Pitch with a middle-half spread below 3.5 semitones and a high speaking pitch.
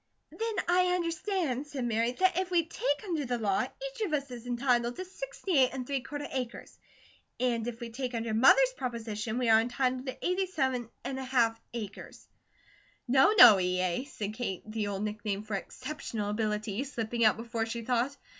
No: average, 4.5 semitones; high, 245 Hz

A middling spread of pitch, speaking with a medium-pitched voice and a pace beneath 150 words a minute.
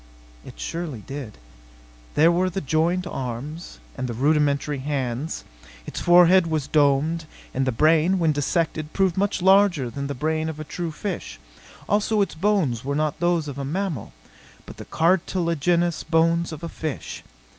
No: average, 3.6 semitones; medium, 160 Hz; average, 160 wpm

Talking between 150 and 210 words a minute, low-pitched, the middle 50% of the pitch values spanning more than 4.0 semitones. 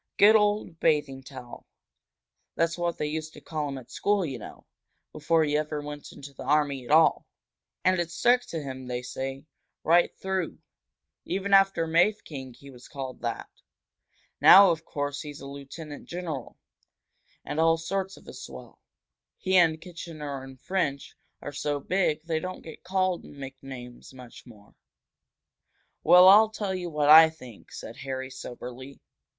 No: average, 160 wpm; medium, 150 Hz; average, 4.5 semitones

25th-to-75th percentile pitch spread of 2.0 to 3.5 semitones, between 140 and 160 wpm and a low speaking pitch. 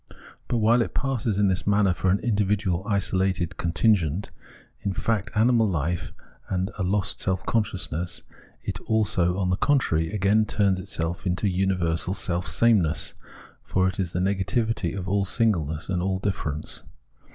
Yes: average, 2.9 semitones; average, 150 wpm; very low, 95 Hz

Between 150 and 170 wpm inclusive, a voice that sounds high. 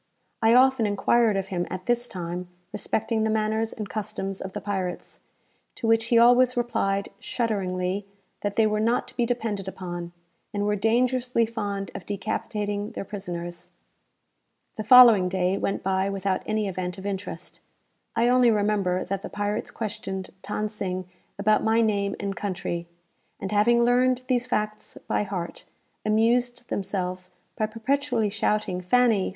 Yes: average, 155 wpm; high, 210 Hz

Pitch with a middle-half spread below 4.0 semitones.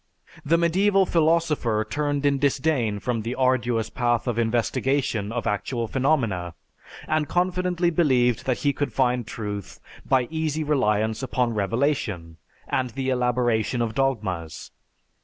No: average, 4.6 semitones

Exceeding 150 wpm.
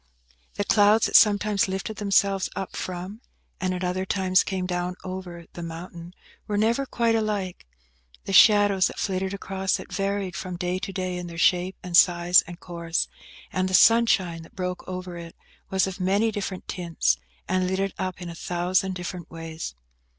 Yes: average, 180 wpm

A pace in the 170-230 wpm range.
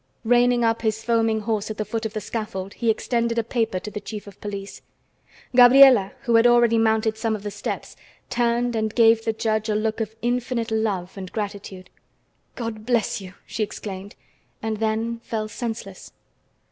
Yes: average, 180 wpm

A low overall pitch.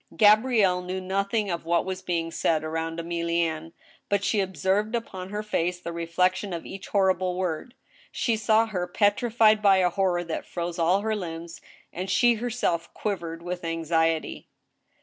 No: medium, 185 Hz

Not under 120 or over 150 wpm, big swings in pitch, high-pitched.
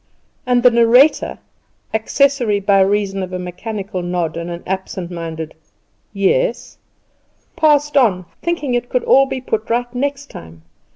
Yes: average, 140 wpm; wide, 6.2 semitones; high, 215 Hz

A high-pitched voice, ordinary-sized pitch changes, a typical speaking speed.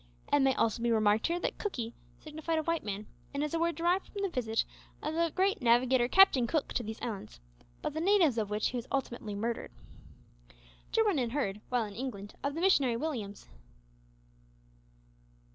No: very high, 260 Hz; wide, 6.5 semitones; average, 185 wpm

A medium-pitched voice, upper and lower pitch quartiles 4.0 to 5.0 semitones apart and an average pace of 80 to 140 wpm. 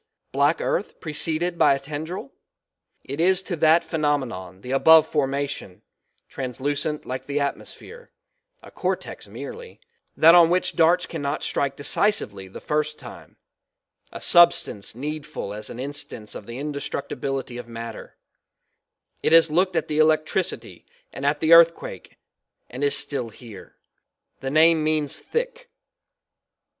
No: medium, 150 Hz; average, 3.6 semitones; slow, 135 wpm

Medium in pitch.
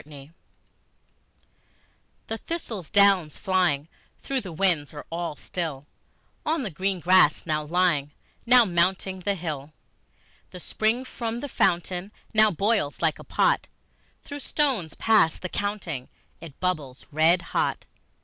Yes: medium, 180 Hz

